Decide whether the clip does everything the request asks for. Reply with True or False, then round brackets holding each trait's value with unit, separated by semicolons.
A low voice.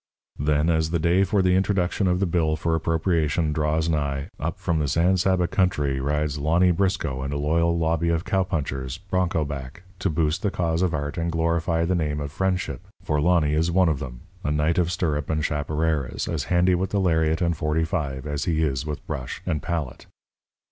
True (80 Hz)